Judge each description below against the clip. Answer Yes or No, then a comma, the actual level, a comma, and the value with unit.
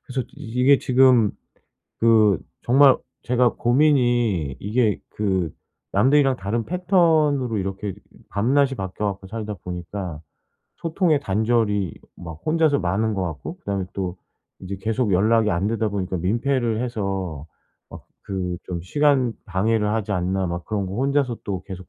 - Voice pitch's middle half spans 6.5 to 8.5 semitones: No, average, 5.1 semitones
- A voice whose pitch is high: No, low, 110 Hz